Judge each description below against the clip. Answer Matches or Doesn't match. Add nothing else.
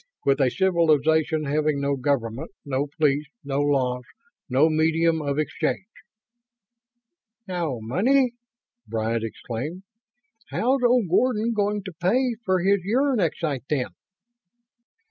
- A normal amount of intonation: Doesn't match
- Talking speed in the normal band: Doesn't match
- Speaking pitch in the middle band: Matches